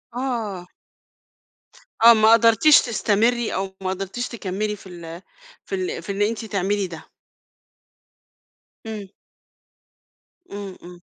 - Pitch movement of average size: Yes, average, 3.3 semitones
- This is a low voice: No, high, 205 Hz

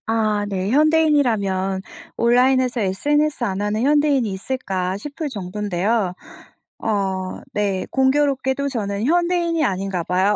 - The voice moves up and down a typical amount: No, wide, 6.3 semitones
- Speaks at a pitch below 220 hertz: No, high, 225 Hz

